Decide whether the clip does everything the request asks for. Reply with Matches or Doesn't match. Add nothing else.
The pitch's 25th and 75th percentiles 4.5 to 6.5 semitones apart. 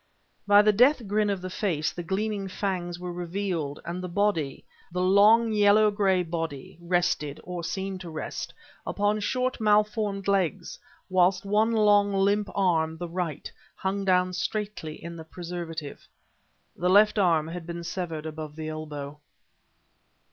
Doesn't match